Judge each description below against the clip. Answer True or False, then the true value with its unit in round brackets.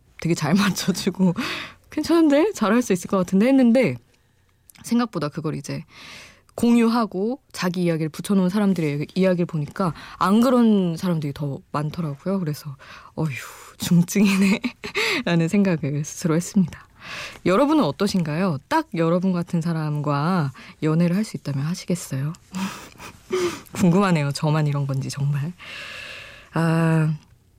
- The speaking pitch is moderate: True (175 Hz)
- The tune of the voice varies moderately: True (5.0 semitones)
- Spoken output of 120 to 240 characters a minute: False (295 characters per minute)